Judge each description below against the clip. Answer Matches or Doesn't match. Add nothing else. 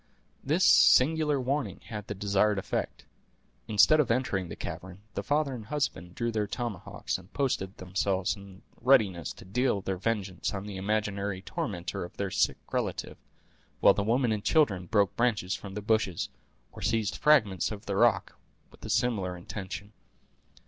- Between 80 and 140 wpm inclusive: Doesn't match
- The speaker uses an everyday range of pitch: Matches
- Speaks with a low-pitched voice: Matches